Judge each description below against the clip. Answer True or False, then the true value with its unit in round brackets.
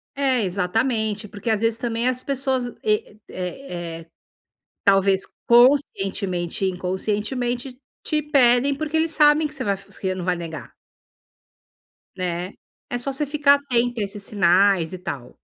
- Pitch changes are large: True (6.0 semitones)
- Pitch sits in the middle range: False (220 Hz)